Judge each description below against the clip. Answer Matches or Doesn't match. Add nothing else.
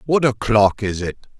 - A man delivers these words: Matches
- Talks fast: Doesn't match